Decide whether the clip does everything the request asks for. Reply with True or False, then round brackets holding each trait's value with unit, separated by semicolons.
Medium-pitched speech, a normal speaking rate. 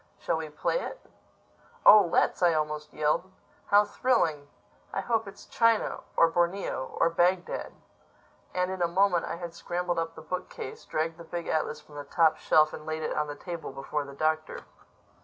True (165 Hz; 175 wpm)